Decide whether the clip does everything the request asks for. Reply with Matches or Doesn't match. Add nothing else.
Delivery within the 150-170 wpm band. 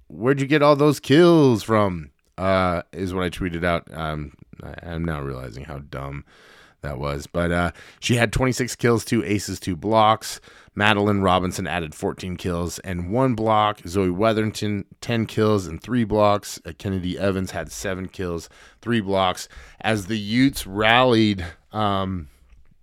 Matches